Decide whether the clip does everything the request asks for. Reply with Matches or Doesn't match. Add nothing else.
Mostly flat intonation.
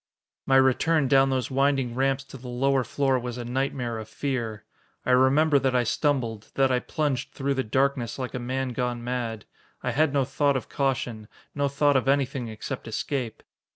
Matches